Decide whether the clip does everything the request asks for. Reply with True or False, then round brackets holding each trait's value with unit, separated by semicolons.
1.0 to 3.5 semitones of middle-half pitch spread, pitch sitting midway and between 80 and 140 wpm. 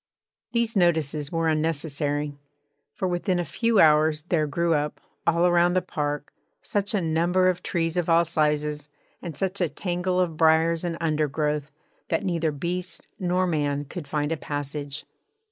False (2.8 semitones; 165 Hz; 160 wpm)